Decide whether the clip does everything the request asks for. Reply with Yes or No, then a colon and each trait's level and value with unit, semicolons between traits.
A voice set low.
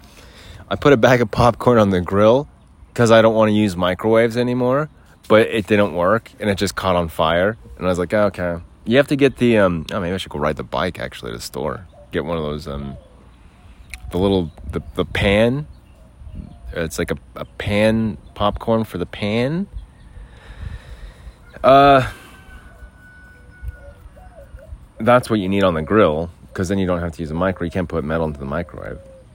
Yes: very low, 95 Hz